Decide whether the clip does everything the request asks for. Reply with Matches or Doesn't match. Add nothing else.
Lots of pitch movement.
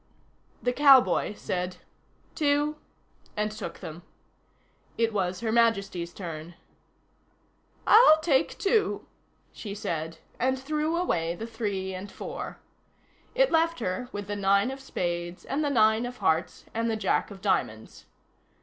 Matches